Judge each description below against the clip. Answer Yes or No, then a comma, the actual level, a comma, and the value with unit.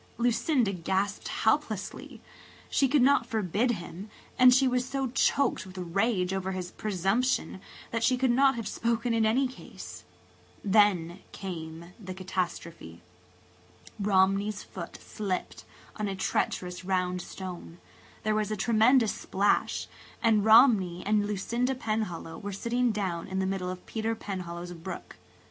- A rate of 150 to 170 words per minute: No, slow, 135 wpm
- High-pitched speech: Yes, high, 205 Hz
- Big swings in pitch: No, average, 4.2 semitones